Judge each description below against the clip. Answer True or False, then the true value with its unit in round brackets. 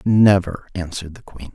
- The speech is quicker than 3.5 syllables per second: True (5.0 syllables/s)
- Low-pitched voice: True (95 Hz)